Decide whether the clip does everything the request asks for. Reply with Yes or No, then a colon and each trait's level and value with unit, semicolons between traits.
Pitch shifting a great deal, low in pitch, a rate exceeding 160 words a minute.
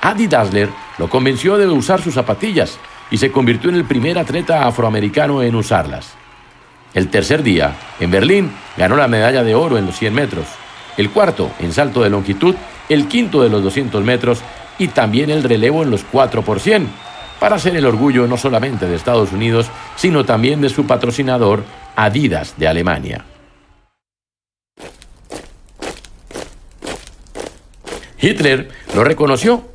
No: wide, 5.9 semitones; low, 125 Hz; average, 145 wpm